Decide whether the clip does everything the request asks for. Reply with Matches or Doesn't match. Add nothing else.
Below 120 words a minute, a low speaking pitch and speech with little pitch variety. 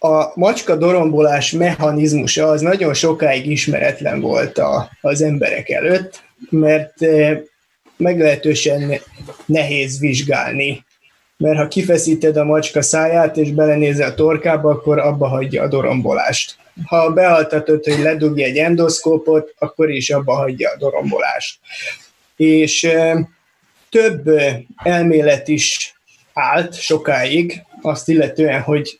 Doesn't match